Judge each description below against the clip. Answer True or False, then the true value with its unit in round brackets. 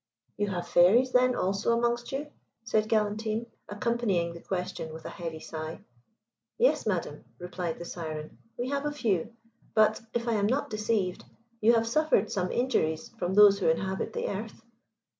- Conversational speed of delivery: True (165 wpm)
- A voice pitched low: False (210 Hz)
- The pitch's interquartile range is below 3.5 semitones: False (4.9 semitones)